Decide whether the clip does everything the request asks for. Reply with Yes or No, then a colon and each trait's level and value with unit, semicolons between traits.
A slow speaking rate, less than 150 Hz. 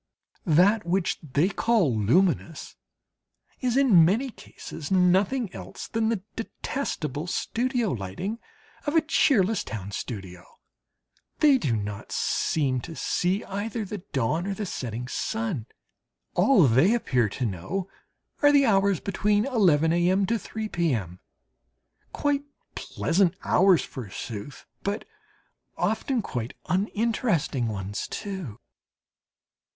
No: slow, 115 wpm; medium, 185 Hz